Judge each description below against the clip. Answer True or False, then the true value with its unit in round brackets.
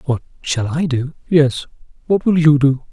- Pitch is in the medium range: True (145 Hz)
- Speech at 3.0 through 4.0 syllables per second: False (4.4 syllables/s)